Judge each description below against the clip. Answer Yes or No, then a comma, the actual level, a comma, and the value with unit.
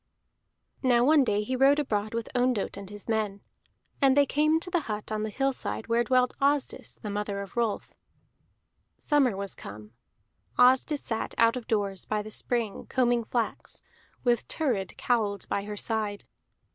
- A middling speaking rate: Yes, average, 165 wpm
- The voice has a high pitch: Yes, high, 230 Hz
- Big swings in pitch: No, average, 3.9 semitones